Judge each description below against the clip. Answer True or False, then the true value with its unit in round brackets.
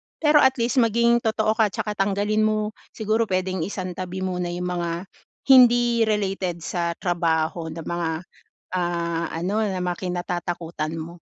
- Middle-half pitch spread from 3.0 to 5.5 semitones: True (3.9 semitones)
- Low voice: False (185 Hz)